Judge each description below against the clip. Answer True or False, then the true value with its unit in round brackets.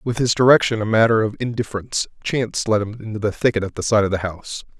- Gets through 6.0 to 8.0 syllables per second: True (6.8 syllables/s)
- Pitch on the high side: False (110 Hz)